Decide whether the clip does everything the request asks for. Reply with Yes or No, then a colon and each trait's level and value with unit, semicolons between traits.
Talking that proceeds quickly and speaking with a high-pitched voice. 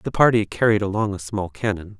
No: fast, 210 wpm; low, 100 Hz